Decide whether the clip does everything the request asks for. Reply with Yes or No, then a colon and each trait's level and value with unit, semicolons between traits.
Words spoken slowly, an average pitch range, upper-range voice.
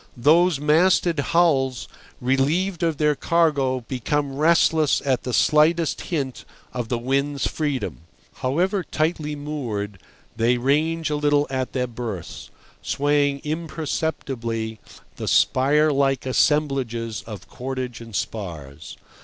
No: slow, 115 wpm; average, 3.8 semitones; medium, 140 Hz